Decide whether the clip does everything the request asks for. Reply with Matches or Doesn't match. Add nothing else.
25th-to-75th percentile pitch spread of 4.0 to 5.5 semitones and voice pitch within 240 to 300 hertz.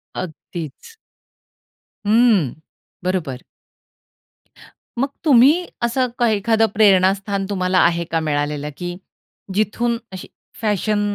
Doesn't match